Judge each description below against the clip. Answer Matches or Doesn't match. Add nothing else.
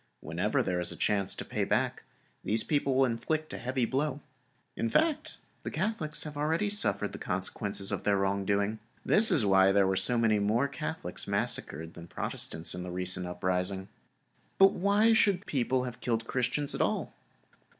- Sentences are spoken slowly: Doesn't match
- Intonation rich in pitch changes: Matches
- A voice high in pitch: Doesn't match